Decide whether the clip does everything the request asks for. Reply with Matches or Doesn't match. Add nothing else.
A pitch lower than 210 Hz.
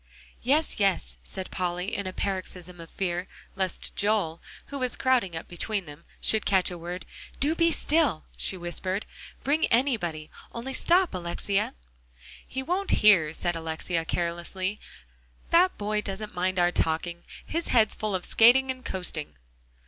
Matches